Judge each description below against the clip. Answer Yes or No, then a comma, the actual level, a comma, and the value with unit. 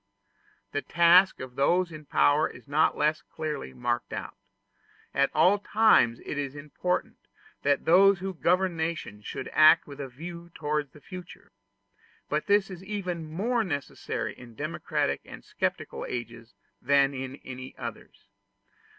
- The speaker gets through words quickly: No, average, 145 wpm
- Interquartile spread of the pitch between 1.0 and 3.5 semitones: No, average, 4.6 semitones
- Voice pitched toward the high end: No, medium, 155 Hz